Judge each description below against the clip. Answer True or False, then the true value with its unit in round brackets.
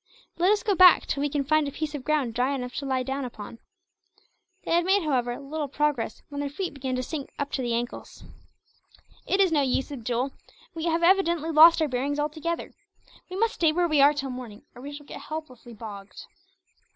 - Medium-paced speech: False (210 wpm)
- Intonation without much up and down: False (4.1 semitones)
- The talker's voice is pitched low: False (285 Hz)